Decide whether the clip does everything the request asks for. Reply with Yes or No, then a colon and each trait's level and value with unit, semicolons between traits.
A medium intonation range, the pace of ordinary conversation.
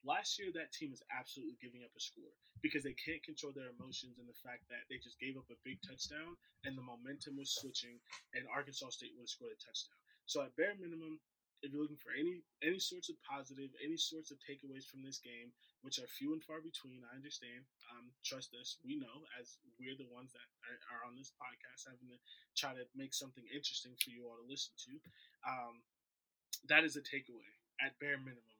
No: average, 3.7 semitones; fast, 215 wpm